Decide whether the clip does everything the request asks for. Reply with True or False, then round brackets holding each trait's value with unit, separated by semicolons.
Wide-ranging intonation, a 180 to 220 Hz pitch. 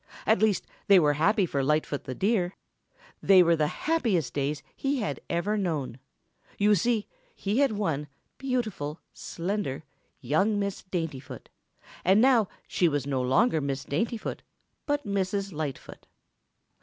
True (6.2 semitones; 185 Hz)